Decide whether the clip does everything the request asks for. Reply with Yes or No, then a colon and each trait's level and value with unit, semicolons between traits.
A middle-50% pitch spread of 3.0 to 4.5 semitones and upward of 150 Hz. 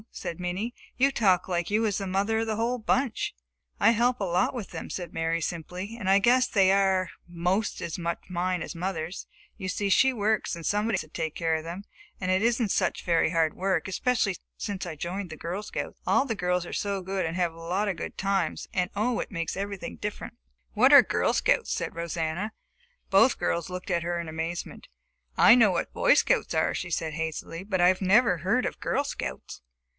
Yes: average, 3.5 semitones; medium, 185 Hz